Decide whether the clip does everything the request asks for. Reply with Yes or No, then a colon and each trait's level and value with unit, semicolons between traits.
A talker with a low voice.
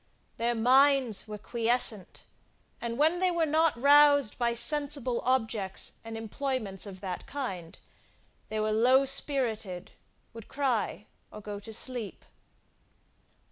No: high, 235 Hz